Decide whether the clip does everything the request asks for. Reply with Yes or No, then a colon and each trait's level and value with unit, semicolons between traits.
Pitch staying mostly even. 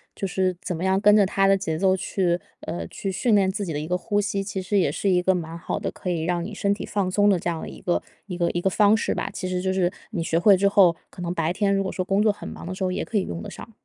Yes: narrow, 2.2 semitones